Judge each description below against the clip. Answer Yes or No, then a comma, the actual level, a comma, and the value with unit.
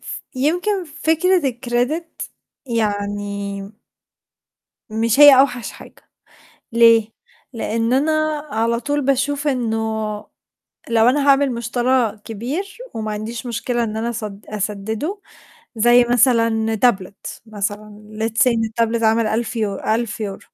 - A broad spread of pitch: No, average, 3.2 semitones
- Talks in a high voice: Yes, high, 230 Hz